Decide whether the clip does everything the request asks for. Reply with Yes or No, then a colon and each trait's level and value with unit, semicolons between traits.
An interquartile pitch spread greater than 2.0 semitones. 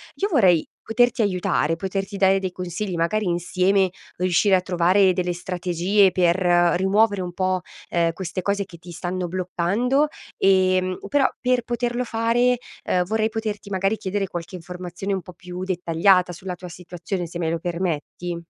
Yes: narrow, 2.4 semitones